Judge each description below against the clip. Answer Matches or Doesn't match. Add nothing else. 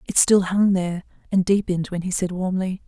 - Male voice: Doesn't match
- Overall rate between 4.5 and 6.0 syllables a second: Matches